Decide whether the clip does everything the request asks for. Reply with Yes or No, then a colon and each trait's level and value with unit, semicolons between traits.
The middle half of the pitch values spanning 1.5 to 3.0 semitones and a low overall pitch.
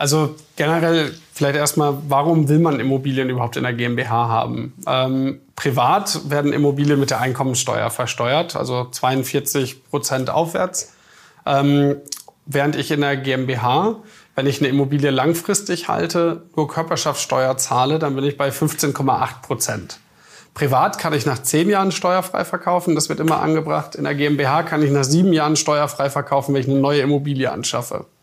No: average, 2.7 semitones; medium, 145 Hz